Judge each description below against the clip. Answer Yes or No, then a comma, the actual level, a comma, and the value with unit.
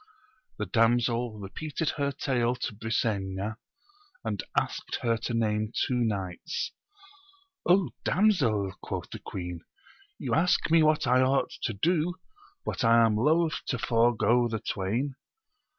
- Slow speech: Yes, slow, 130 wpm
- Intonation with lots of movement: No, average, 4.4 semitones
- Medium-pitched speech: No, low, 115 Hz